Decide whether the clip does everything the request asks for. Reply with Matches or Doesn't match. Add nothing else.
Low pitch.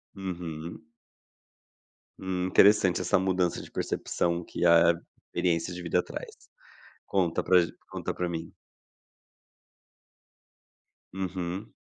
Matches